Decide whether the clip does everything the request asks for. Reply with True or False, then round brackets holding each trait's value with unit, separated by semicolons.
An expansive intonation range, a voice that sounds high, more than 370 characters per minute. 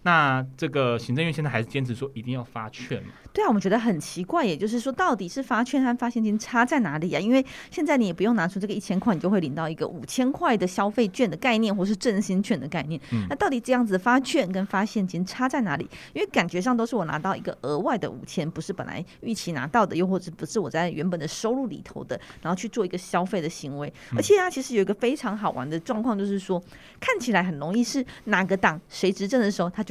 True (6.0 semitones; 200 Hz; 385 characters per minute)